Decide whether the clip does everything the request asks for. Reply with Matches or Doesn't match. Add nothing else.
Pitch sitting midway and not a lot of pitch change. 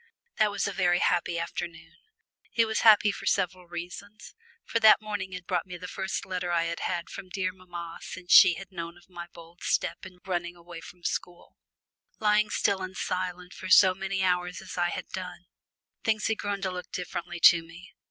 Matches